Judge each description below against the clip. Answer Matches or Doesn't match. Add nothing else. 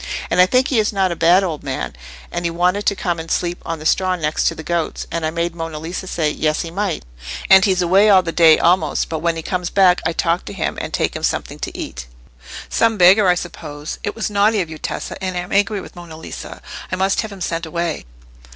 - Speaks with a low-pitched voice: Doesn't match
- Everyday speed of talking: Doesn't match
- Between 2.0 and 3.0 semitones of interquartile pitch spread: Matches